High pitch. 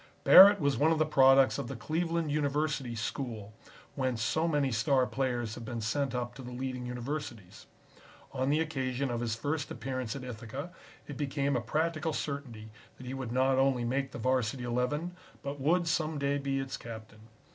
No: low, 135 Hz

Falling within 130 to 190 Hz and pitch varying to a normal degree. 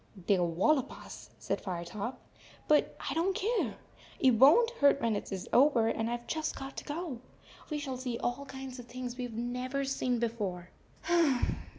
No: very high, 250 Hz; average, 3.7 semitones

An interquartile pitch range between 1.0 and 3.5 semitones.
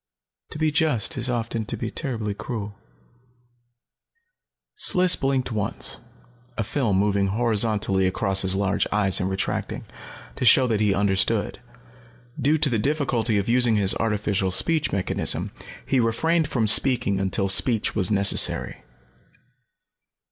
No: average, 4.2 semitones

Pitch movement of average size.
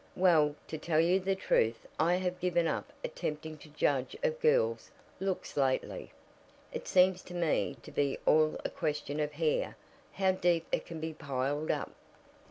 Yes: average, 3.6 semitones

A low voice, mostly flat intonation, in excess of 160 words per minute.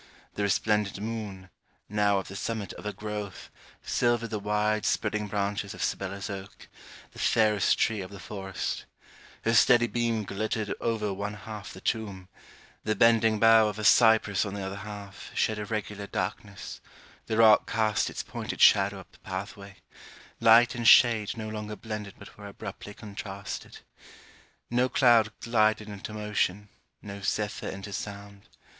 No: low, 105 Hz; narrow, 1.6 semitones; average, 155 wpm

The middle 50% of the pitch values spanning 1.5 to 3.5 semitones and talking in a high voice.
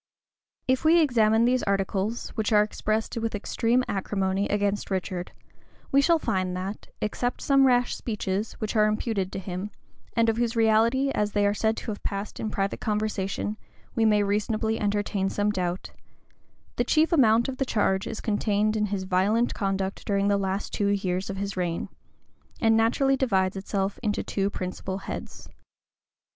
Yes: narrow, 2.6 semitones; high, 210 Hz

